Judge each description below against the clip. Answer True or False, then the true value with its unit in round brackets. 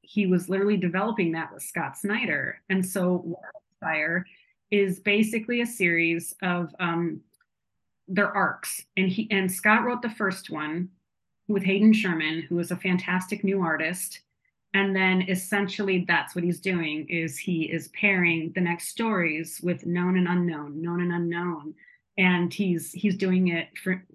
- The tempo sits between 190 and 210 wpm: False (155 wpm)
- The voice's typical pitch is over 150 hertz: True (185 Hz)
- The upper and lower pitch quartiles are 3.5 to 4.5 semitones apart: False (2.4 semitones)